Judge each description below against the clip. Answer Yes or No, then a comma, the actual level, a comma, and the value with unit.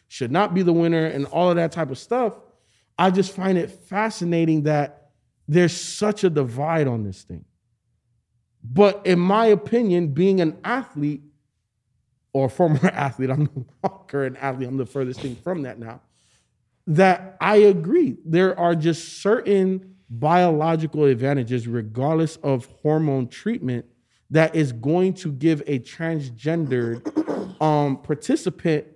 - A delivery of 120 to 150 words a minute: Yes, average, 145 wpm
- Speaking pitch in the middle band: Yes, medium, 155 Hz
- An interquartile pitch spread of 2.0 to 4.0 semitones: No, wide, 5.6 semitones